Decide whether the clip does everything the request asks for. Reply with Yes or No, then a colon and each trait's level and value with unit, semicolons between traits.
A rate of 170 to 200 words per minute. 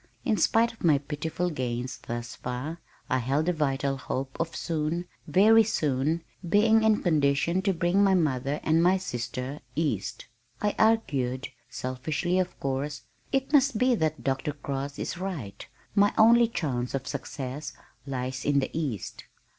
No: average, 155 wpm